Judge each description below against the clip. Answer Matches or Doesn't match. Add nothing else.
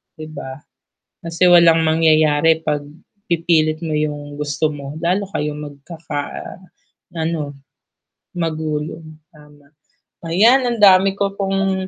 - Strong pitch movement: Doesn't match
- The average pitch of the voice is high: Doesn't match